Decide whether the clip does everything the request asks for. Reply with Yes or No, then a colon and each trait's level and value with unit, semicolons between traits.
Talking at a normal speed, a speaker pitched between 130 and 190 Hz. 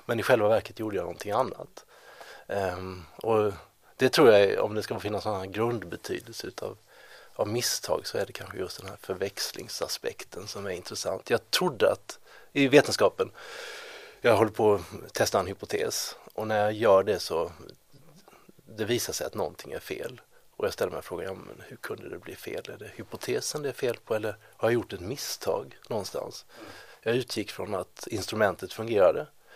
Yes: average, 175 wpm; medium, 140 Hz